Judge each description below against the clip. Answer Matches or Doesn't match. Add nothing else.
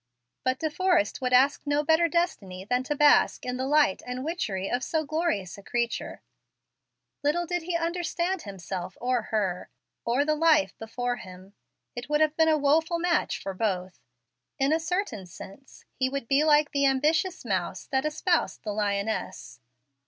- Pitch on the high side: Matches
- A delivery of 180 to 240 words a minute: Doesn't match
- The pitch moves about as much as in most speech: Doesn't match